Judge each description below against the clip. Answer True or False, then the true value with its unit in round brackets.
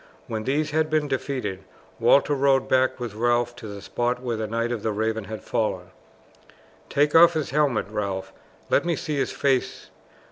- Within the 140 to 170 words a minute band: False (180 wpm)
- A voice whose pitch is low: True (120 Hz)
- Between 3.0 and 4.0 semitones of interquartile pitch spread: False (4.5 semitones)